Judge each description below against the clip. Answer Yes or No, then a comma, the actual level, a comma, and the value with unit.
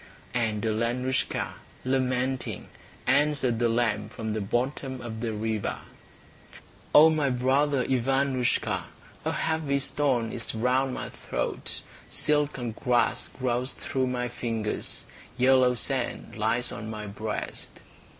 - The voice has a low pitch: Yes, low, 125 Hz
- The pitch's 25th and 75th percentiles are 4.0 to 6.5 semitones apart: No, average, 2.8 semitones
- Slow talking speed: Yes, slow, 115 wpm